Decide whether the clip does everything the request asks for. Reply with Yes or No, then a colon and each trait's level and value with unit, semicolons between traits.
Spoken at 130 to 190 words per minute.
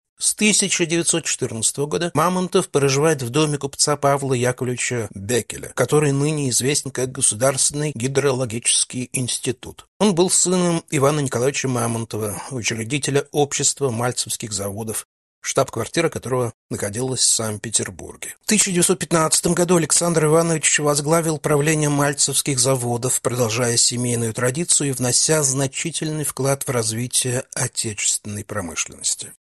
No: slow, 110 wpm